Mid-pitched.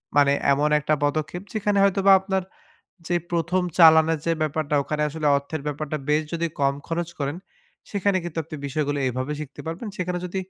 Yes: medium, 160 Hz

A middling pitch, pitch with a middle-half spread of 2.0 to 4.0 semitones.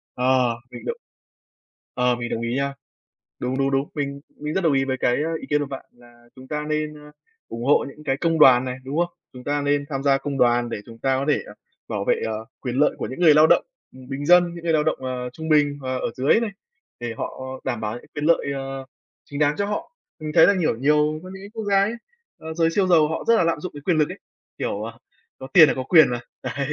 Yes: medium, 145 Hz; average, 3.6 semitones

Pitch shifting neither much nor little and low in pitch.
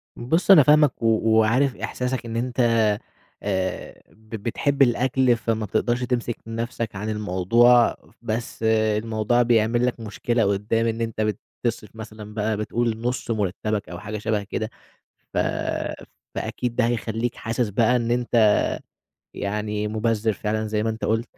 No: narrow, 2.1 semitones; low, 115 Hz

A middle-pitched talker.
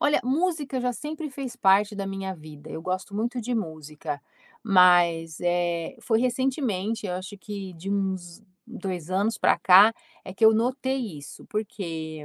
No: high, 195 Hz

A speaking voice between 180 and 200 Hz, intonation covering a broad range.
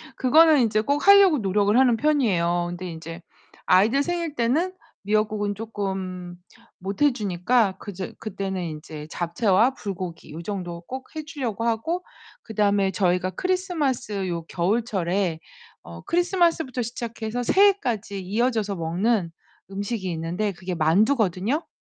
No: high, 210 Hz; wide, 5.7 semitones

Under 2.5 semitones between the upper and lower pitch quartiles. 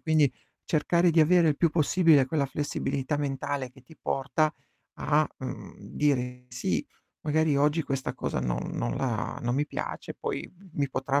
No: average, 2.8 semitones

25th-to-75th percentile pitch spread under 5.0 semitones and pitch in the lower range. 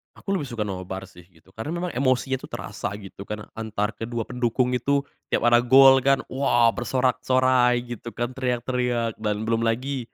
Yes: narrow, 2.6 semitones; low, 120 Hz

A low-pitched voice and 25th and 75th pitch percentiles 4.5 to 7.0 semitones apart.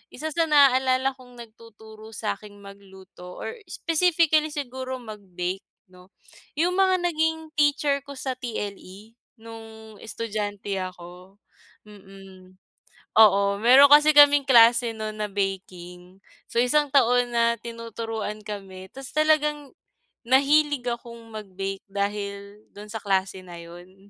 No: high, 220 Hz; wide, 5.4 semitones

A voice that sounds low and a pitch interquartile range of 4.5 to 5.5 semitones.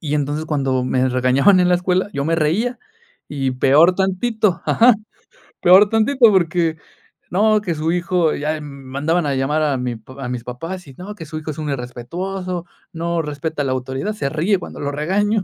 No: medium, 160 Hz; average, 4.9 semitones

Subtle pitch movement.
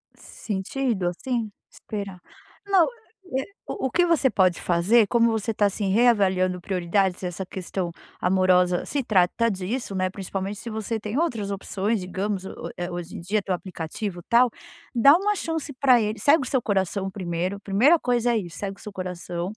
No: average, 4.2 semitones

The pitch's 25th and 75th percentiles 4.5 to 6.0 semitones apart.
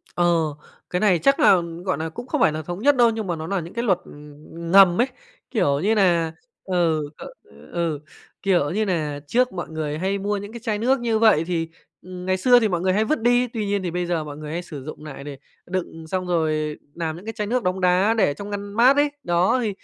Yes: average, 5.0 semitones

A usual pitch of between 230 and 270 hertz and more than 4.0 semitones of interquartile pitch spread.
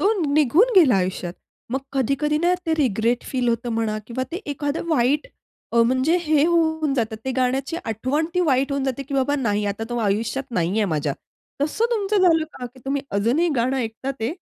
Yes: very high, 265 Hz; average, 4.7 semitones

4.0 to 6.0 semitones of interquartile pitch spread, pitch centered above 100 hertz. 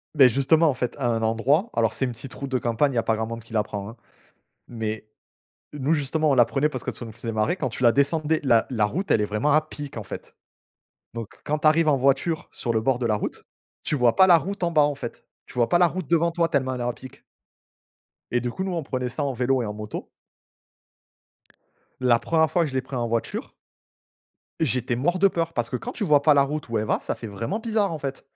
Yes: average, 5.0 semitones; low, 130 Hz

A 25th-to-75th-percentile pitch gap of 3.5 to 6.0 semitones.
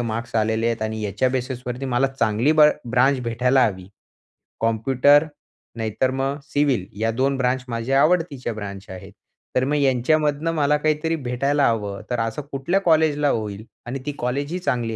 Yes: average, 4.0 semitones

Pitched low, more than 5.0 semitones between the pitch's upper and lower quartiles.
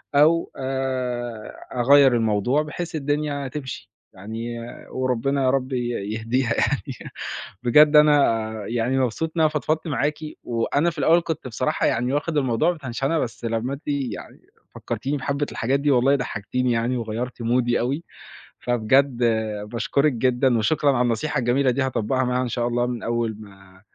No: low, 130 Hz; average, 3.1 semitones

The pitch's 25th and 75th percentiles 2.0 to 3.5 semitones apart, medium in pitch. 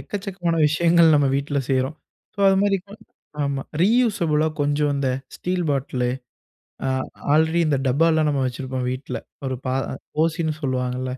No: average, 4.1 semitones; medium, 150 Hz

